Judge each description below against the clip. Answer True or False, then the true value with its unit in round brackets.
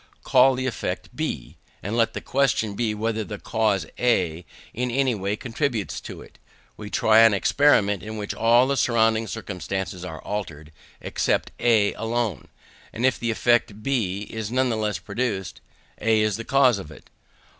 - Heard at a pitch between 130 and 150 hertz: False (110 Hz)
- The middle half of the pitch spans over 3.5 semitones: False (3.0 semitones)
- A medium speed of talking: True (160 wpm)